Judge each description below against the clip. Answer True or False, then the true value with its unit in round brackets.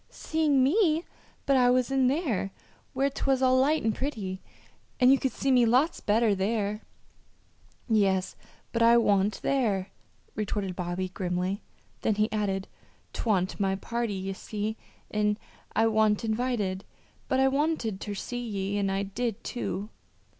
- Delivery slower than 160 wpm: True (150 wpm)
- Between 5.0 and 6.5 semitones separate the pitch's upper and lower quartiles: False (4.6 semitones)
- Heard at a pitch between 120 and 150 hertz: False (220 Hz)